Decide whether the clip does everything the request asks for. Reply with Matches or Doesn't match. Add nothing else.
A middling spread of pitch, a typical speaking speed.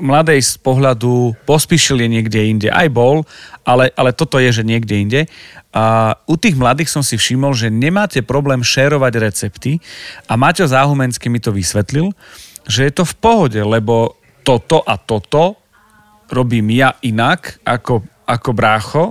Matches